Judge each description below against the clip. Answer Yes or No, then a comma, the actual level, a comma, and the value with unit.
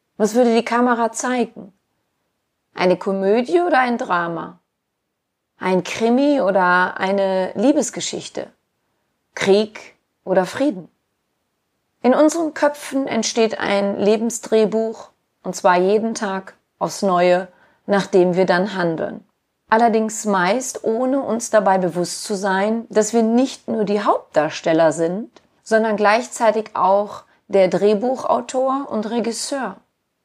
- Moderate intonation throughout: Yes, average, 4.0 semitones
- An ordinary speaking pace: No, slow, 110 wpm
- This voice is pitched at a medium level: No, high, 215 Hz